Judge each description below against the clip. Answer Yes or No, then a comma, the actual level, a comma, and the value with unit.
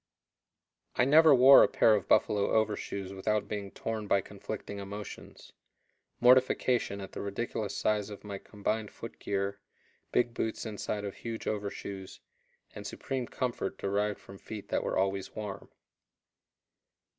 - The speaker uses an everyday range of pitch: No, narrow, 2.3 semitones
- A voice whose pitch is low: Yes, low, 105 Hz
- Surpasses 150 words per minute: No, average, 140 wpm